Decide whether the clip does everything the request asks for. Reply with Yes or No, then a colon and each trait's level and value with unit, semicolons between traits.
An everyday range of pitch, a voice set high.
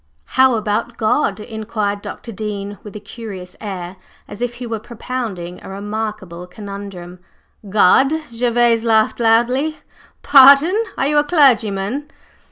Yes: average, 3.5 semitones; high, 220 Hz